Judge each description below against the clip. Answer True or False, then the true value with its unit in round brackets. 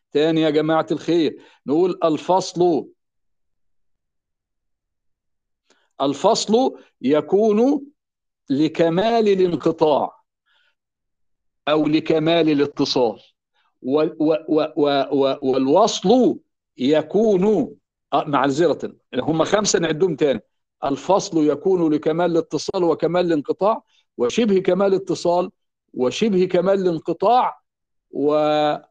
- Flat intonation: False (4.6 semitones)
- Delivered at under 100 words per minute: True (70 wpm)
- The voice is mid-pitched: True (160 Hz)